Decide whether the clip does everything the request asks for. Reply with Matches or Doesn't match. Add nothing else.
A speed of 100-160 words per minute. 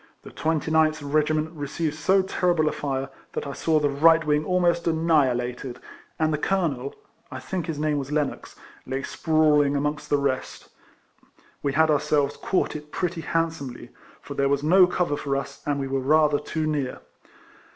Doesn't match